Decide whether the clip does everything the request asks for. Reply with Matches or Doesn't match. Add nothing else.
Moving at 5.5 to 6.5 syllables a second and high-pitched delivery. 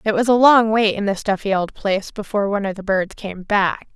Matches